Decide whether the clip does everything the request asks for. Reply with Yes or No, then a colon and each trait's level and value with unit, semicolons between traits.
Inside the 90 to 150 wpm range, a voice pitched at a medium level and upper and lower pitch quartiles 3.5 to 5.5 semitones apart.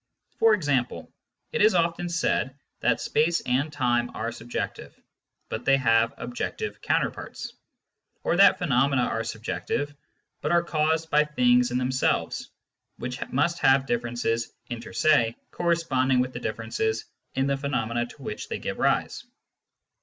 No: average, 140 wpm; low, 130 Hz; average, 4.2 semitones